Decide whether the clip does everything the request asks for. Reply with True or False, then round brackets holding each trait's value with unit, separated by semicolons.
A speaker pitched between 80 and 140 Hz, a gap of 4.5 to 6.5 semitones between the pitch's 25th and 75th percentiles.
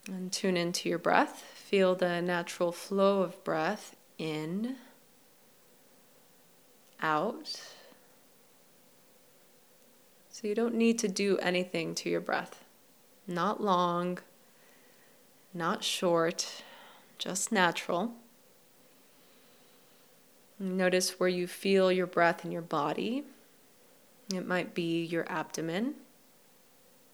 False (185 Hz; 5.2 semitones)